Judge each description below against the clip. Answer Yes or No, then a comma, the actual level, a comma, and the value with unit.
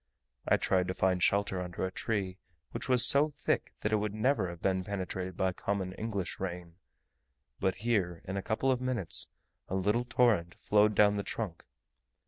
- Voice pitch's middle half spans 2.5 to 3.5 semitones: Yes, average, 2.9 semitones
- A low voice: Yes, low, 100 Hz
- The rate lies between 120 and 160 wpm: No, average, 180 wpm